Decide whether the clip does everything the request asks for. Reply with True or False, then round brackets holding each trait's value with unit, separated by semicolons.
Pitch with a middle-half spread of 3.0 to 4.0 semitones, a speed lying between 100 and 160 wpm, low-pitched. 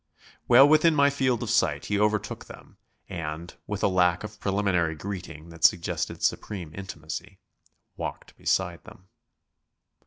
True (3.7 semitones; 135 wpm; 95 Hz)